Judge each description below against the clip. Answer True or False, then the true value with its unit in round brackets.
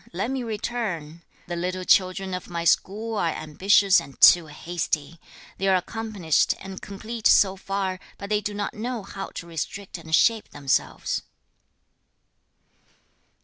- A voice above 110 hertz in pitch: True (190 Hz)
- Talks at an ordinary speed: True (145 wpm)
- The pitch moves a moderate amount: True (3.6 semitones)